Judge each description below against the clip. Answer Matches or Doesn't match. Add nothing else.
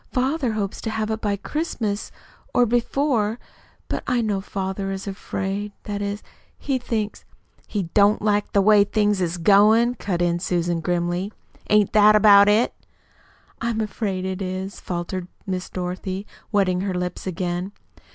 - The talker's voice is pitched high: Matches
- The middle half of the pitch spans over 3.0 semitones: Doesn't match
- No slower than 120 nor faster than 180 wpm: Matches